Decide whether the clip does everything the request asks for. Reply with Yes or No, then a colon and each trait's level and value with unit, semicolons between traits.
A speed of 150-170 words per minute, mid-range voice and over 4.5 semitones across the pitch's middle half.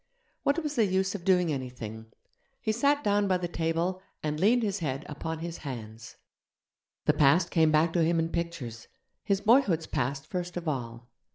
No: average, 180 wpm; medium, 170 Hz; average, 5.2 semitones